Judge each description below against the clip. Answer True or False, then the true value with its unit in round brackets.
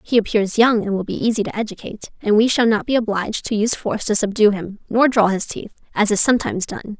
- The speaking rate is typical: False (250 wpm)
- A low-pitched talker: False (215 Hz)